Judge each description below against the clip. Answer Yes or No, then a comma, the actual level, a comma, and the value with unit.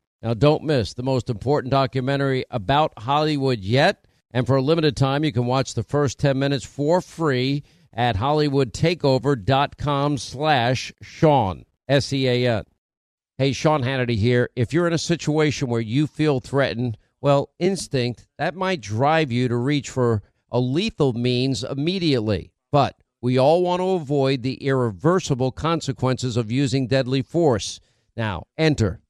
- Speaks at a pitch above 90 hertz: Yes, low, 135 Hz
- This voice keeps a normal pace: Yes, average, 145 wpm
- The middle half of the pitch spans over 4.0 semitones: No, average, 3.1 semitones